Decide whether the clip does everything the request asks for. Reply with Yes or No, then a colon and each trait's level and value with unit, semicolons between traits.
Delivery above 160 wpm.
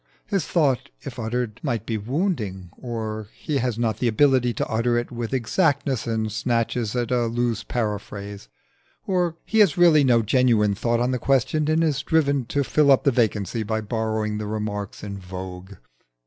Yes: average, 175 wpm